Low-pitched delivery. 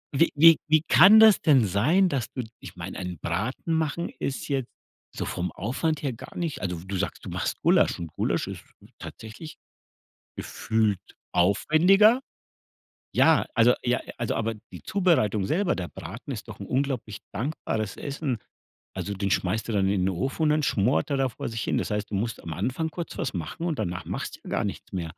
Yes: low, 120 Hz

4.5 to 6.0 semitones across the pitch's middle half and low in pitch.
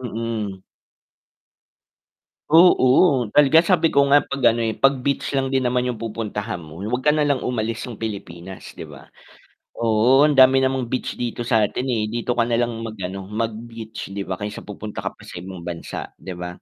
No: average, 3.8 semitones; low, 115 Hz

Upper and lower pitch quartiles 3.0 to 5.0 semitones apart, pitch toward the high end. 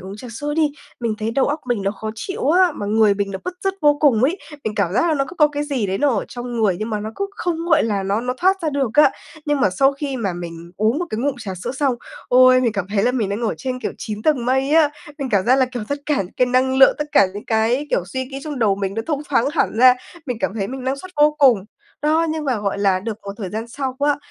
No: wide, 5.5 semitones; very high, 250 Hz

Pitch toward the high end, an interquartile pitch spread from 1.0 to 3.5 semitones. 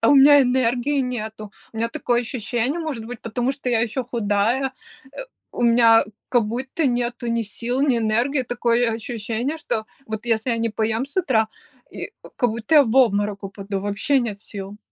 Yes: high, 235 Hz; narrow, 2.6 semitones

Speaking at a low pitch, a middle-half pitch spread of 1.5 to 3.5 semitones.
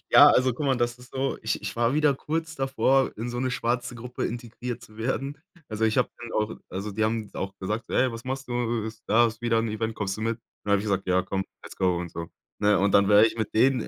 Yes: low, 115 Hz; average, 2.9 semitones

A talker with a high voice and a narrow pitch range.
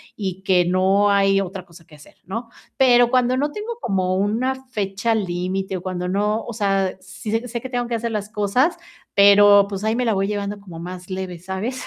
No: high, 200 Hz; average, 3.5 semitones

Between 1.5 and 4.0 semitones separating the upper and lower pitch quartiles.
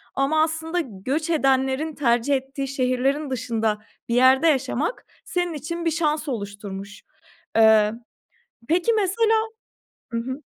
No: average, 4.9 semitones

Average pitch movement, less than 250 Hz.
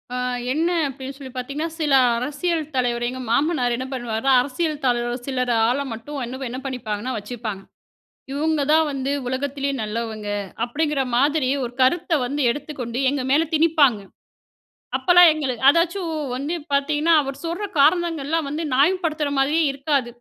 No: average, 3.7 semitones; very high, 275 Hz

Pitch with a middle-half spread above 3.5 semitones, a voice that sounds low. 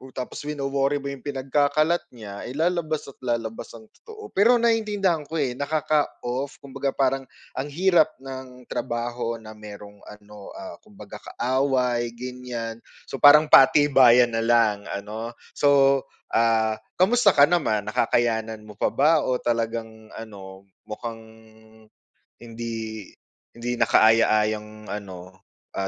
Yes: average, 4.4 semitones; low, 120 Hz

